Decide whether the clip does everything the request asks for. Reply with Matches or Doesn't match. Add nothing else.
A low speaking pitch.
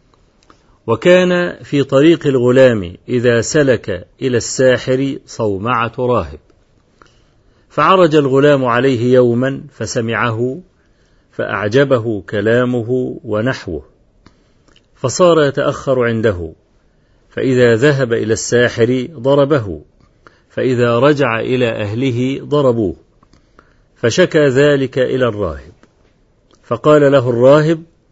Matches